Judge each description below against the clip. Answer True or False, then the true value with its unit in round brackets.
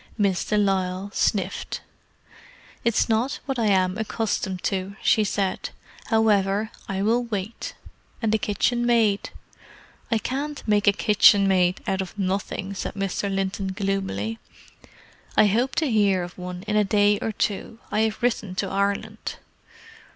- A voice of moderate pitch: False (200 Hz)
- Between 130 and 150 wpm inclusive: True (145 wpm)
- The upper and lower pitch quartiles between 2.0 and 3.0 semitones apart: True (2.4 semitones)